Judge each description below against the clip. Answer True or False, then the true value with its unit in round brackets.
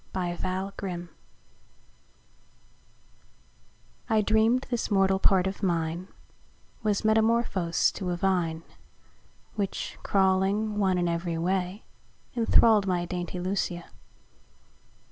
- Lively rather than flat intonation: False (2.8 semitones)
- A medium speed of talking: False (100 wpm)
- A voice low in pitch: False (190 Hz)